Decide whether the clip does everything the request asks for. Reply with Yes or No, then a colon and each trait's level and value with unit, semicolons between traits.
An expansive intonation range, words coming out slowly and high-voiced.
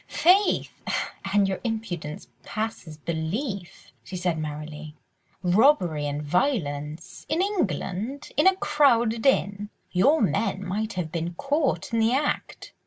Yes: wide, 8.1 semitones; slow, 115 wpm; high, 200 Hz